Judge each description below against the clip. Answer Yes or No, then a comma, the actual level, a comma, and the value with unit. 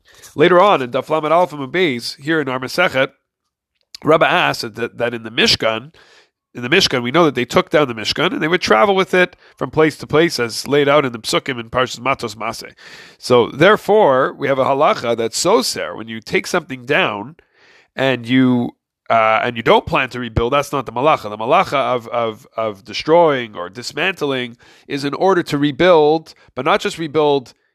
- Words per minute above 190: Yes, average, 200 wpm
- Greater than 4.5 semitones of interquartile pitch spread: Yes, average, 4.9 semitones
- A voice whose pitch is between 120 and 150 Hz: Yes, low, 135 Hz